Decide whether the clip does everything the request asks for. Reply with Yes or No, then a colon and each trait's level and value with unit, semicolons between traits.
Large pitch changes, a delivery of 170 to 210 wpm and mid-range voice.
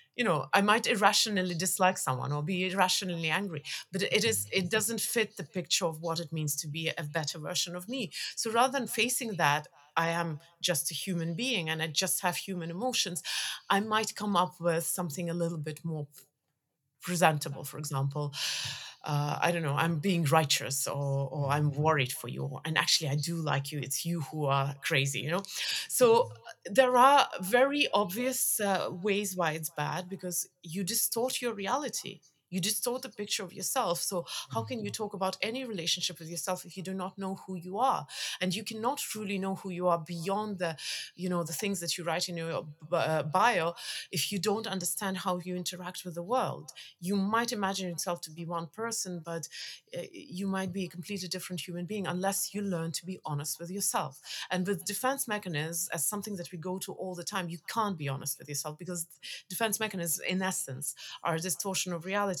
No: average, 3.7 semitones; average, 200 wpm; medium, 180 Hz